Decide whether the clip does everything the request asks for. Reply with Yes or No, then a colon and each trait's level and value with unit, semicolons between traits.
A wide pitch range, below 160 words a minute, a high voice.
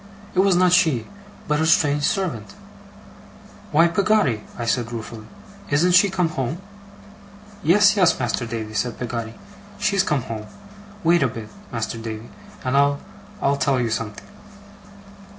No: wide, 7.1 semitones; average, 145 wpm; medium, 140 Hz